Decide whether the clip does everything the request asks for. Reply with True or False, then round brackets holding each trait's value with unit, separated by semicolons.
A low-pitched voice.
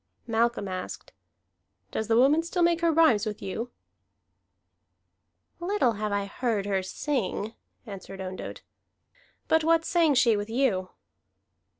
False (230 Hz)